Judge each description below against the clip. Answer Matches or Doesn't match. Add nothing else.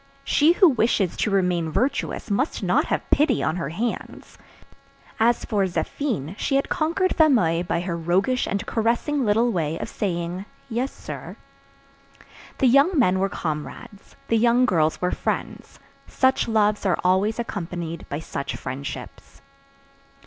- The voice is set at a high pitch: Matches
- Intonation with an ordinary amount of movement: Doesn't match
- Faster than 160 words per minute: Doesn't match